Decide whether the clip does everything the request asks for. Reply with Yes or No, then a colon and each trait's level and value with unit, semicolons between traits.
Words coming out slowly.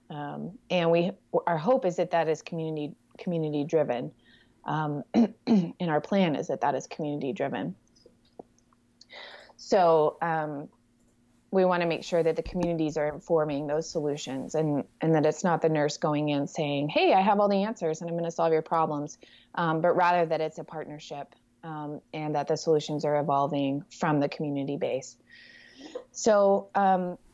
No: average, 175 wpm